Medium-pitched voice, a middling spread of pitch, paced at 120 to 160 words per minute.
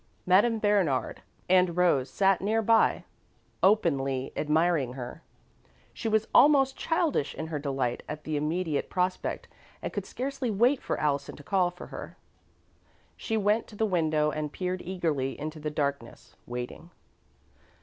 No: medium, 175 Hz; wide, 6.0 semitones; average, 145 wpm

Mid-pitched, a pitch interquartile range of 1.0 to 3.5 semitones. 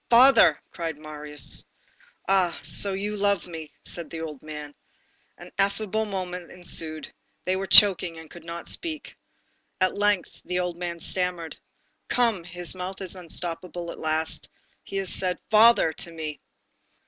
Yes: medium, 180 Hz; average, 3.1 semitones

